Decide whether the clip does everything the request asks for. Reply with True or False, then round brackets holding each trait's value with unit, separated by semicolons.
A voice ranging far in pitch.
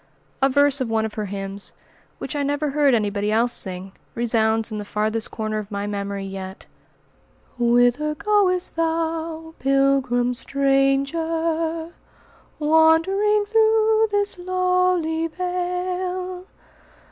True (8.0 semitones)